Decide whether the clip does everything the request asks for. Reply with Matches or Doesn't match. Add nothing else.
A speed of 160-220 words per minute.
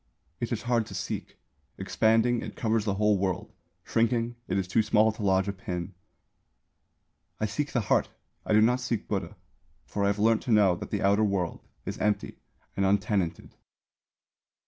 Matches